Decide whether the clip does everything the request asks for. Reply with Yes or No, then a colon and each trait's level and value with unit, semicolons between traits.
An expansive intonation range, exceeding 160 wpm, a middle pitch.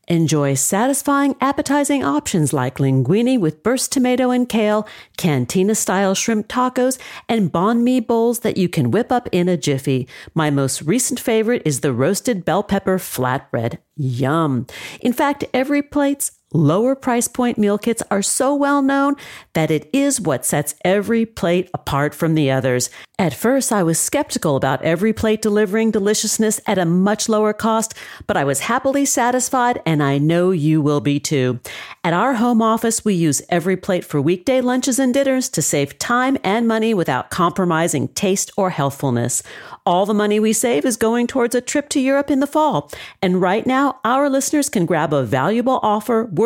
No: wide, 7.8 semitones; average, 175 wpm; high, 210 Hz